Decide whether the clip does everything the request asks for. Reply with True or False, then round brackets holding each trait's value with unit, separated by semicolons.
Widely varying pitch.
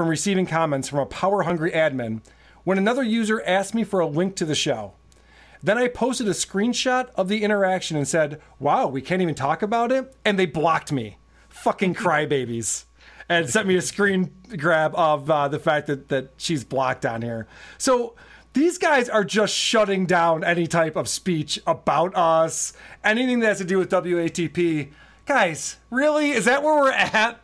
True (6.0 semitones)